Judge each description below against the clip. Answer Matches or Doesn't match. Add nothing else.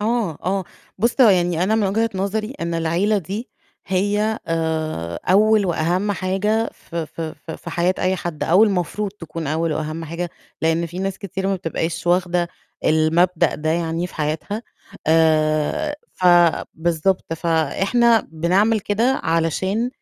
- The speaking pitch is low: Doesn't match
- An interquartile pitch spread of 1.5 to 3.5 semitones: Doesn't match